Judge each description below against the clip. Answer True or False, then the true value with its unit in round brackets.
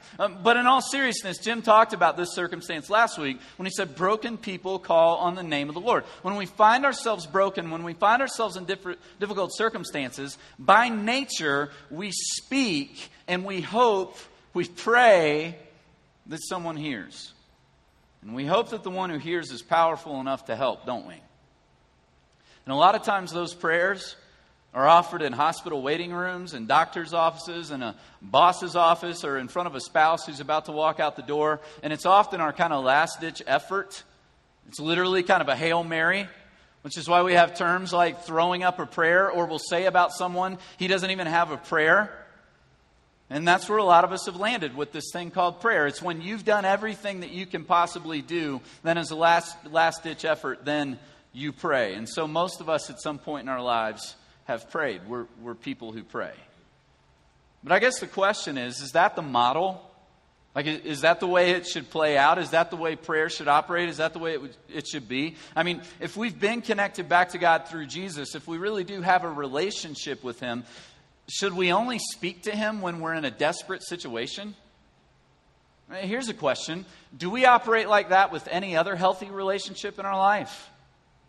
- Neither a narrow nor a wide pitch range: True (4.0 semitones)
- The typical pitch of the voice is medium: True (175 Hz)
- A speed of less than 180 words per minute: False (200 wpm)